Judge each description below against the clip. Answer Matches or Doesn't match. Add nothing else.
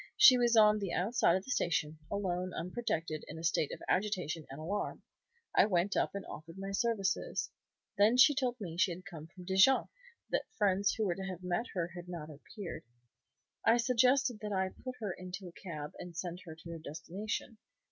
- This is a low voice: Doesn't match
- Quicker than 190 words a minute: Matches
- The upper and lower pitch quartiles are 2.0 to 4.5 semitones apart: Matches